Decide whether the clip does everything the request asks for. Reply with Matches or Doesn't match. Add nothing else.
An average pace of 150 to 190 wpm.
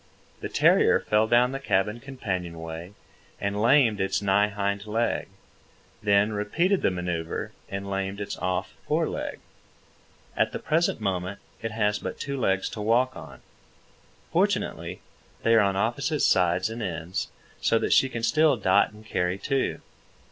Matches